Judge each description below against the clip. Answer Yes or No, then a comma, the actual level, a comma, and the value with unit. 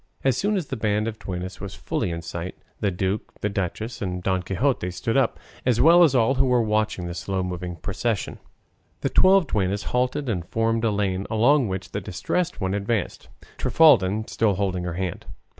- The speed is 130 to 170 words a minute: No, average, 190 wpm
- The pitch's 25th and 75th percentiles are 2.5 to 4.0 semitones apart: No, average, 4.8 semitones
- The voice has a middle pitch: No, low, 105 Hz